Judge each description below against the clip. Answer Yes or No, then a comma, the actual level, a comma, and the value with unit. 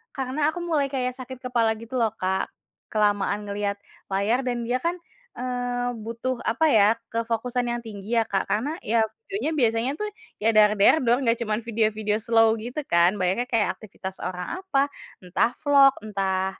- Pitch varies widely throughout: No, average, 3.3 semitones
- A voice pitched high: Yes, high, 230 Hz